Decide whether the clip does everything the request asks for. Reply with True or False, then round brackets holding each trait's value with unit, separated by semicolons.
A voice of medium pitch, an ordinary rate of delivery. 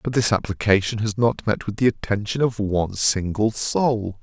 False (105 Hz; 185 wpm)